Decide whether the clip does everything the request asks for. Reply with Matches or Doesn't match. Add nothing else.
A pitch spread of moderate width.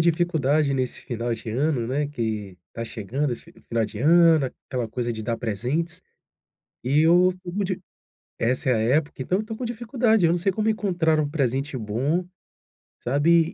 Doesn't match